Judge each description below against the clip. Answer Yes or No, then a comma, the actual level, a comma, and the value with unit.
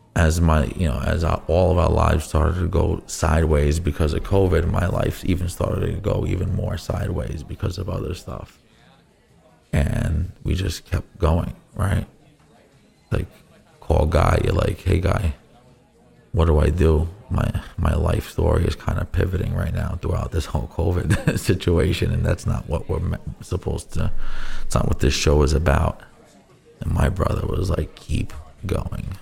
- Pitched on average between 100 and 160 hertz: No, very low, 90 Hz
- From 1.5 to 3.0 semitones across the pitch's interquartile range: No, average, 4.0 semitones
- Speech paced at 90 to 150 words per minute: No, average, 170 wpm